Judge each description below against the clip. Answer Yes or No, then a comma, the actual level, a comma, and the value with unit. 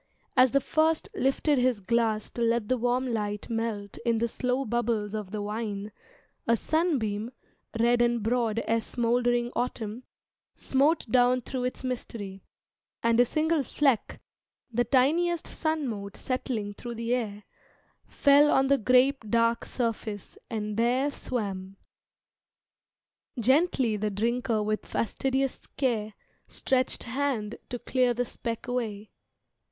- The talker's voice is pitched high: Yes, high, 235 Hz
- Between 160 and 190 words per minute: No, slow, 135 wpm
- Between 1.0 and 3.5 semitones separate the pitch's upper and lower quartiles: Yes, average, 3.0 semitones